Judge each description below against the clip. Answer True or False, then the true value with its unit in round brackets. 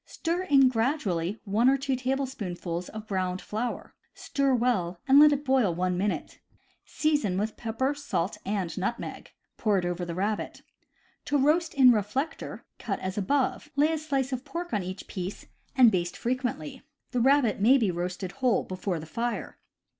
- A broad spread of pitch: True (6.4 semitones)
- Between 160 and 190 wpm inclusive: True (170 wpm)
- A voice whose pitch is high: True (230 Hz)